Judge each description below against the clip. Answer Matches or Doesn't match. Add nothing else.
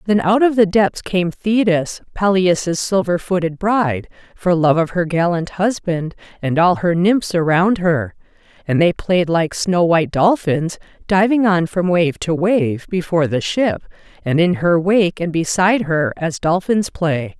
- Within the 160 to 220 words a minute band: Matches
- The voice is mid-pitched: Matches